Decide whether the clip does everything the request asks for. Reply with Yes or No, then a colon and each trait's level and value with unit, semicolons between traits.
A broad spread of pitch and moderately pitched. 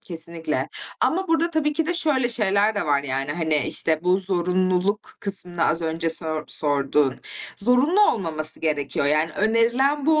Yes: wide, 7.8 semitones; medium, 180 Hz